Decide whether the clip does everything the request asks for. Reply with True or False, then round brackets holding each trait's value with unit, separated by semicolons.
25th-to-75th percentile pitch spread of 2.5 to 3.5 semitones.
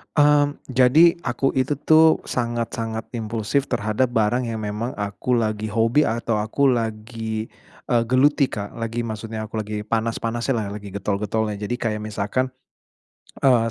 True (2.9 semitones)